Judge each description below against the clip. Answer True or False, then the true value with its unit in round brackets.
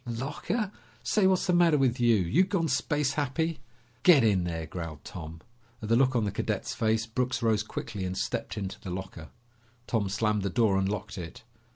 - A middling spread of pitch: False (6.9 semitones)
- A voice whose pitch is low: True (115 Hz)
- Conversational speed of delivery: True (195 wpm)